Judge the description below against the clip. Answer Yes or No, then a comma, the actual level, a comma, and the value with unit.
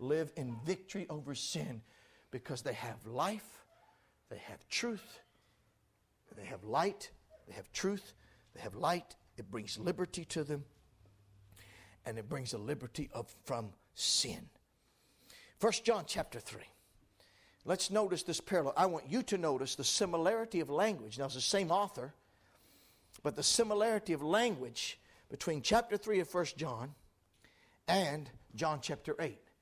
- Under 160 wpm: Yes, average, 145 wpm